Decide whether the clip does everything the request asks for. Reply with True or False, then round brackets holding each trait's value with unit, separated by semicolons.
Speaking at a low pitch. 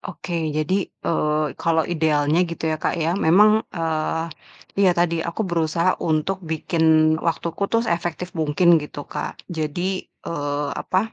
False (165 Hz)